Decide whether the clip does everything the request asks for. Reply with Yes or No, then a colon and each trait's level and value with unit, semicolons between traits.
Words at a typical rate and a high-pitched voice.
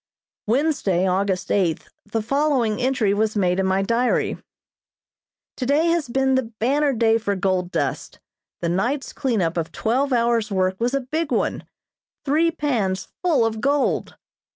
Yes: average, 150 wpm; high, 230 Hz